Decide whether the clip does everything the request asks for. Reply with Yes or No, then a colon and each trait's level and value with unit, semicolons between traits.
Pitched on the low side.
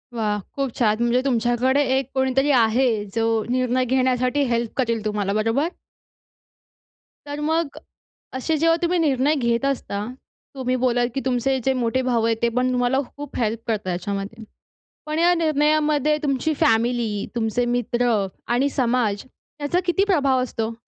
No: very high, 255 Hz